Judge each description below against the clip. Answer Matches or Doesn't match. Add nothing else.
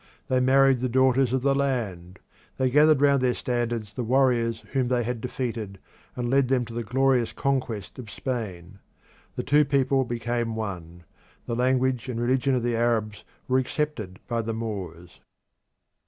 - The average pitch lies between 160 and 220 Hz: Doesn't match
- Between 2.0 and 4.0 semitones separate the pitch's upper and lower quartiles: Matches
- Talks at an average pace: Matches